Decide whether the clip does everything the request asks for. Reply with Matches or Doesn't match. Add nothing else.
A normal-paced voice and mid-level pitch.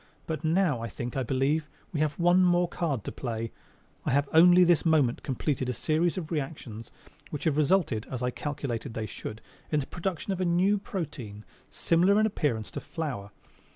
Matches